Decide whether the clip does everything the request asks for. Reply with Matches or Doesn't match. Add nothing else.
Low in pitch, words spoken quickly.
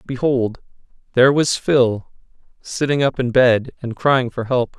Doesn't match